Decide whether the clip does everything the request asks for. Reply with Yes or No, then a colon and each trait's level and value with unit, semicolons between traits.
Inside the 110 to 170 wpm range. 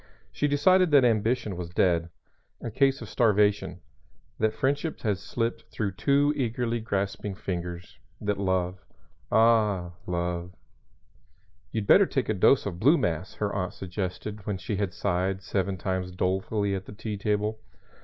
Yes: average, 150 wpm